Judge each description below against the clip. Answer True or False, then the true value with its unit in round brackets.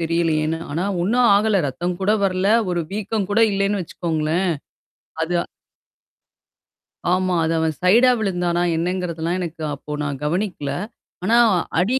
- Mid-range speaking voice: True (180 Hz)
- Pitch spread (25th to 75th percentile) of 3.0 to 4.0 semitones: True (3.4 semitones)